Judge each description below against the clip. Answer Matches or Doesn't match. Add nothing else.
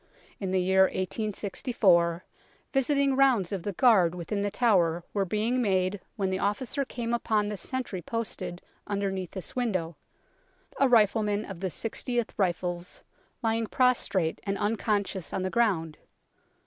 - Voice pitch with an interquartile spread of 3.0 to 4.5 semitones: Matches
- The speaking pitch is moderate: Doesn't match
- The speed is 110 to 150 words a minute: Matches